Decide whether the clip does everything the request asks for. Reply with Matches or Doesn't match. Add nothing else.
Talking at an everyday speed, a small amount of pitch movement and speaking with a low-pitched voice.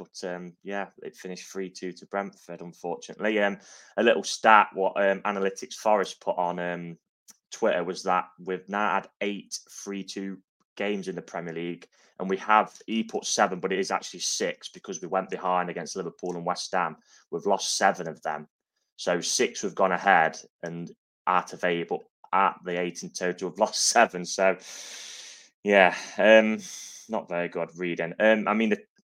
Matches